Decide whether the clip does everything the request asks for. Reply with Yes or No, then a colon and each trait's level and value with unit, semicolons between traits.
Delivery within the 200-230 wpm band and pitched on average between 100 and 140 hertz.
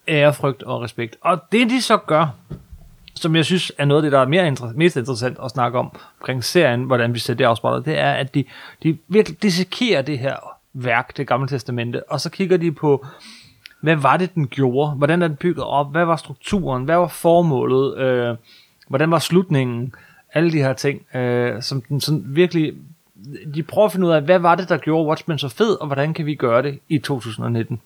No: average, 210 wpm; medium, 150 Hz